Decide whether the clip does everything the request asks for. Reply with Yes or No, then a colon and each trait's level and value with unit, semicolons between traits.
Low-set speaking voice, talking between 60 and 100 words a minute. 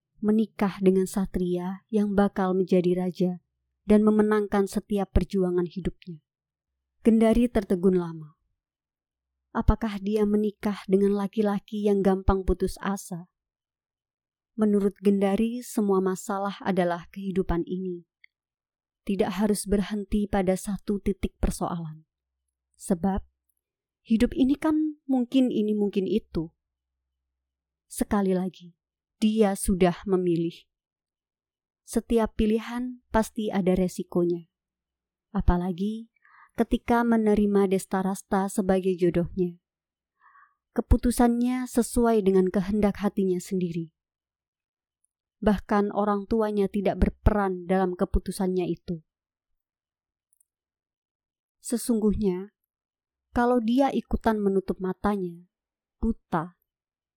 No: high, 195 Hz; slow, 85 wpm